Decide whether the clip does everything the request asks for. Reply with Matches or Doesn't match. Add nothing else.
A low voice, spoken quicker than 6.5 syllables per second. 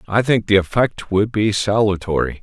Doesn't match